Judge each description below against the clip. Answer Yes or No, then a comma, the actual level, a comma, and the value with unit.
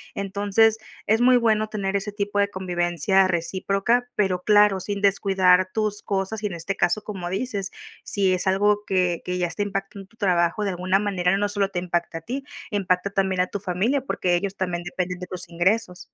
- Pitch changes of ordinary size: No, narrow, 2.2 semitones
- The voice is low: No, high, 195 Hz